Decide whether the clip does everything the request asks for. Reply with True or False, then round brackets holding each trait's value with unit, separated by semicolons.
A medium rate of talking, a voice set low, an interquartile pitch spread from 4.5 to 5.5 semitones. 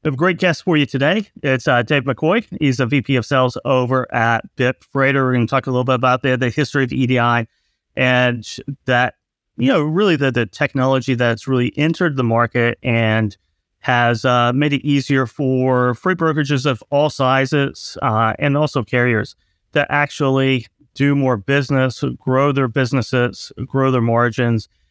False (170 wpm; 130 Hz; 2.7 semitones)